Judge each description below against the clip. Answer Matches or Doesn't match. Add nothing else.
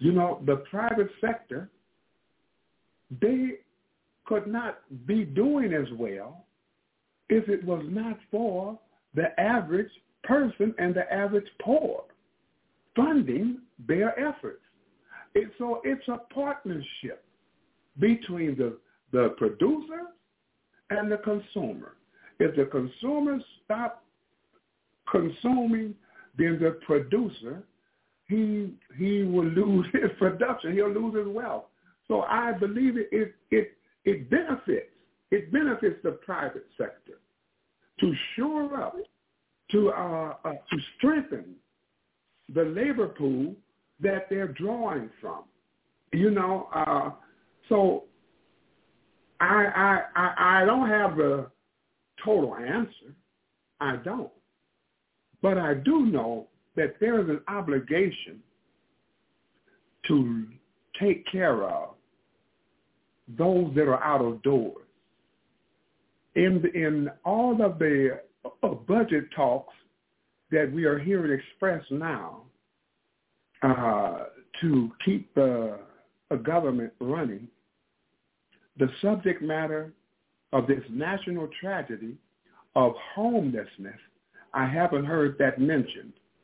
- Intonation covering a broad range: Matches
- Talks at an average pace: Doesn't match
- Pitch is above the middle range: Matches